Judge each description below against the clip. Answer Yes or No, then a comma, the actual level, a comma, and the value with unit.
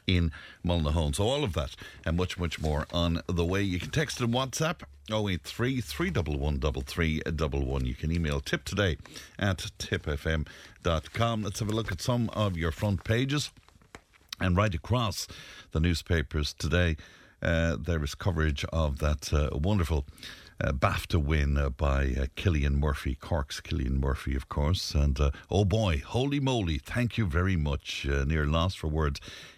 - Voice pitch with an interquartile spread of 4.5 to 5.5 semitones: Yes, average, 5.2 semitones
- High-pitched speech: No, very low, 85 Hz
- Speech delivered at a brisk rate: No, average, 160 wpm